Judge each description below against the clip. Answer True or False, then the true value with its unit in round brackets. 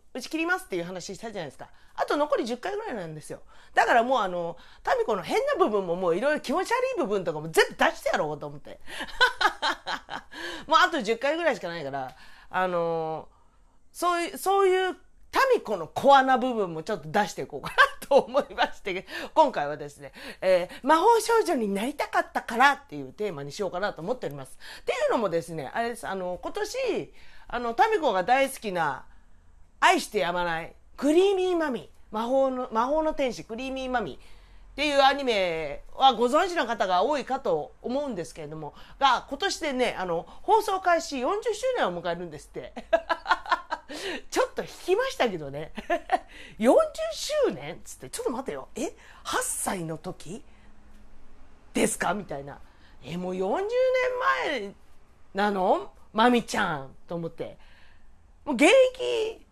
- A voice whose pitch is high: True (255 Hz)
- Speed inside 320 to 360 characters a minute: True (330 characters per minute)